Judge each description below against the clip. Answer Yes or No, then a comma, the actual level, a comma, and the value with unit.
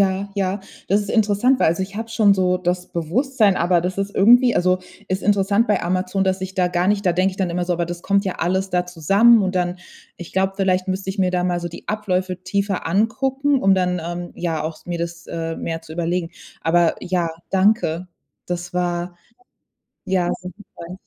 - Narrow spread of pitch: Yes, narrow, 2.2 semitones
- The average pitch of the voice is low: No, medium, 185 Hz